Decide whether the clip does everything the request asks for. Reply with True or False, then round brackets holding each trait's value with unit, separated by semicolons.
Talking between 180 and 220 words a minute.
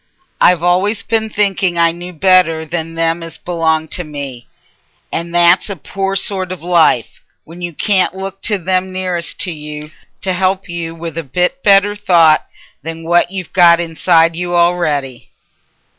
False (165 wpm)